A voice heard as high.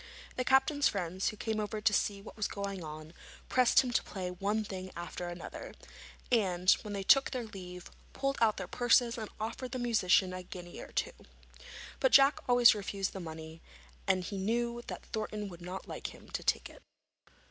Yes: high, 205 Hz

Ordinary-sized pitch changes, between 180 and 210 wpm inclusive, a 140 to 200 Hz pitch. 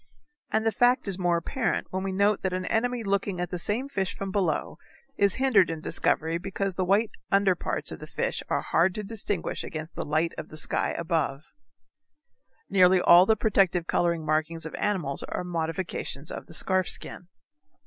Yes: average, 3.3 semitones; average, 190 wpm; medium, 185 Hz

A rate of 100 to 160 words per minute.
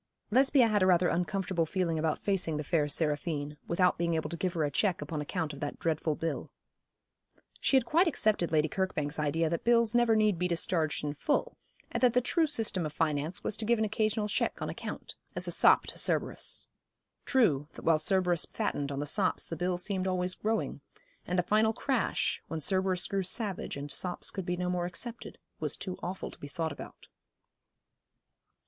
No: average, 200 wpm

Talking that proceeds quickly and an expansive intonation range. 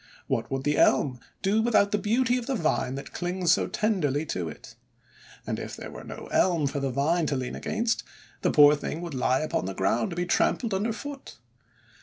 Yes: fast, 215 wpm; wide, 7.5 semitones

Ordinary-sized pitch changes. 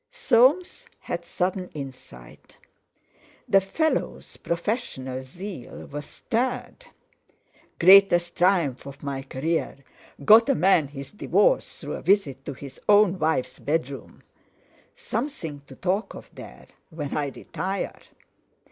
No: wide, 6.9 semitones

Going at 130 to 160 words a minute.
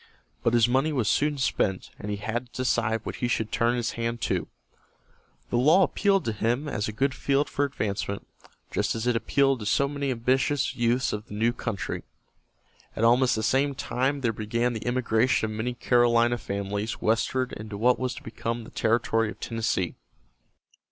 No: average, 185 wpm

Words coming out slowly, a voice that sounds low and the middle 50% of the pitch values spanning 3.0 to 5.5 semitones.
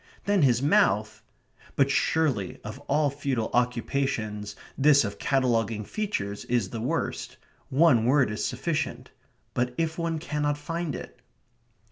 Yes: slow, 130 wpm; low, 130 Hz; average, 5.1 semitones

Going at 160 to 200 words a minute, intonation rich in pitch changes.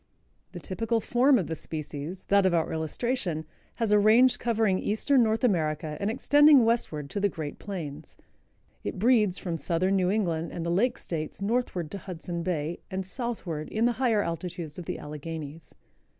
Yes: average, 175 wpm; wide, 5.7 semitones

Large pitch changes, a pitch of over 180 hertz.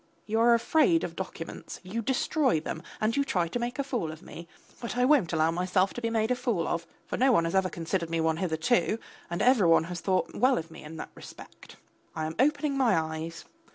Yes: wide, 6.9 semitones; high, 190 Hz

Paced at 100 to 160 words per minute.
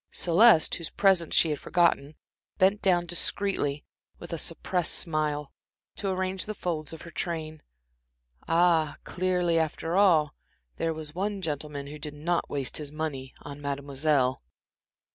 Yes: average, 145 wpm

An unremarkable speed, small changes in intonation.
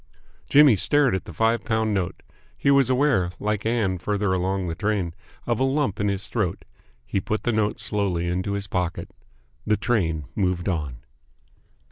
No: average, 170 wpm; average, 3.8 semitones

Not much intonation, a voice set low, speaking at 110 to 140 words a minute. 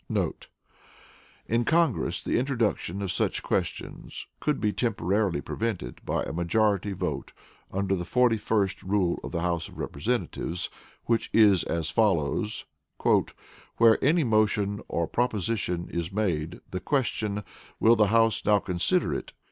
No: average, 4.3 semitones; low, 105 Hz; slow, 135 wpm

